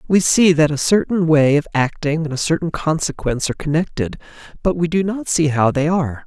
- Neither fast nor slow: No, fast, 210 wpm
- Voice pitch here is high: No, medium, 160 Hz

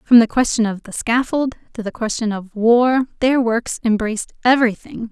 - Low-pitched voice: No, high, 230 Hz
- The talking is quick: No, average, 175 wpm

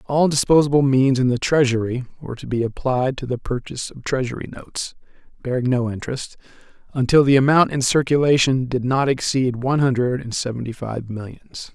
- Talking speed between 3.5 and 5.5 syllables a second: No, 5.7 syllables/s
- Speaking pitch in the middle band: No, low, 130 Hz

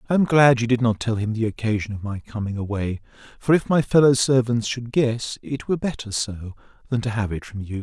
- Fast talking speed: Yes, fast, 255 wpm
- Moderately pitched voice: No, low, 115 Hz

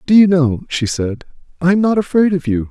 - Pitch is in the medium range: Yes, medium, 160 Hz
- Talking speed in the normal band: No, fast, 245 wpm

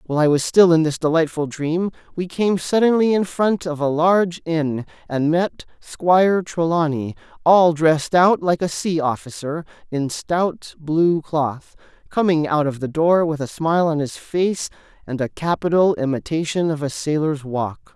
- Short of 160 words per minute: No, average, 170 wpm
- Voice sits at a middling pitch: Yes, medium, 160 Hz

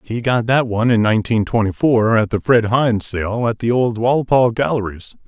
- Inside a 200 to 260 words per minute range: Yes, fast, 205 wpm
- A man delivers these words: Yes, male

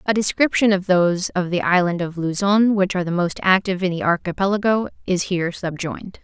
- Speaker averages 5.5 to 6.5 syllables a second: Yes, 6.0 syllables/s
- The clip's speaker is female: Yes, female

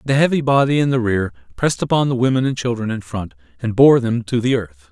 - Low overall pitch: Yes, low, 120 Hz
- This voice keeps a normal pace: No, fast, 245 wpm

